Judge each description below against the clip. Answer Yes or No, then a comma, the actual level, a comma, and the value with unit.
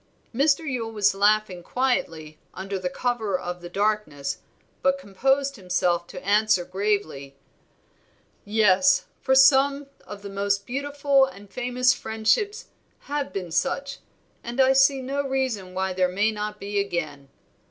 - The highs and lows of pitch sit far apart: Yes, wide, 6.2 semitones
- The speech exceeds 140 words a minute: No, slow, 135 wpm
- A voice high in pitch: Yes, high, 210 Hz